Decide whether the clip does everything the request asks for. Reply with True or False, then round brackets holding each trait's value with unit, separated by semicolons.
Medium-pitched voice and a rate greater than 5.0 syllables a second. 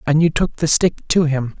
False (155 Hz; 4.8 syllables/s)